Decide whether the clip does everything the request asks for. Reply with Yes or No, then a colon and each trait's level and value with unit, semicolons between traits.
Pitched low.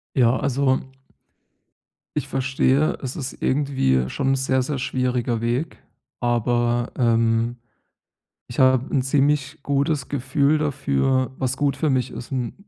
Yes: low, 130 Hz